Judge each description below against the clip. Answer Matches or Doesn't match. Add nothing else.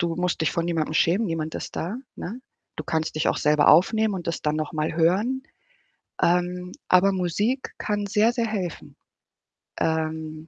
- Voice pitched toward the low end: Doesn't match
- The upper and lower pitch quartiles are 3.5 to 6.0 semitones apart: Matches